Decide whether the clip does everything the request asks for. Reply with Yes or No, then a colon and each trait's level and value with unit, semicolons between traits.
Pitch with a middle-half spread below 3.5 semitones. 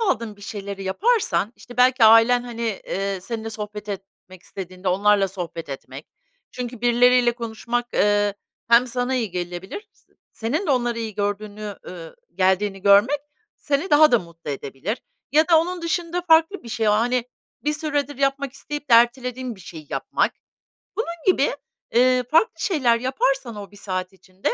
No: average, 5.2 semitones